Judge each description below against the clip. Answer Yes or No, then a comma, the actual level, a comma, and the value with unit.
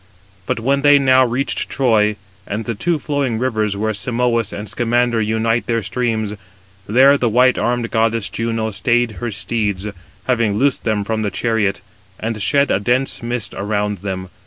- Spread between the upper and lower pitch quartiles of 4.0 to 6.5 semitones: No, narrow, 2.6 semitones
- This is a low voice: Yes, low, 115 Hz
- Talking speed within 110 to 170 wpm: Yes, average, 165 wpm